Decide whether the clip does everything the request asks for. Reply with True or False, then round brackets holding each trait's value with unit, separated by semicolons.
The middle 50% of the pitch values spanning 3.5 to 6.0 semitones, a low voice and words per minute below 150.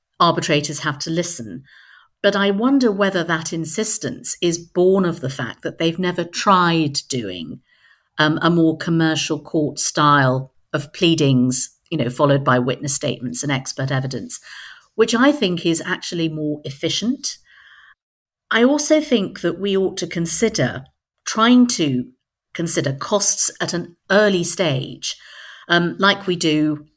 False (4.3 semitones; 165 Hz; 140 wpm)